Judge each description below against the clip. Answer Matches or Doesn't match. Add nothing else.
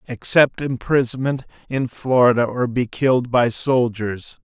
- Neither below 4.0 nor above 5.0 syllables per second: Matches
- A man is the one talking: Matches